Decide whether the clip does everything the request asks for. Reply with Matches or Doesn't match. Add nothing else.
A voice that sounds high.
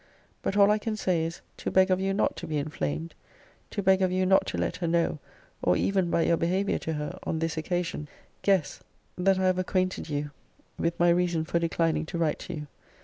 Doesn't match